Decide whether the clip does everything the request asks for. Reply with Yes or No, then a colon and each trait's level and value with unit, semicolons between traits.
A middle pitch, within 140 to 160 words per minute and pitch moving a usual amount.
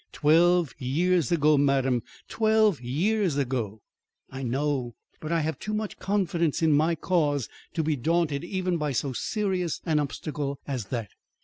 Yes: medium, 155 Hz; average, 150 wpm; average, 4.3 semitones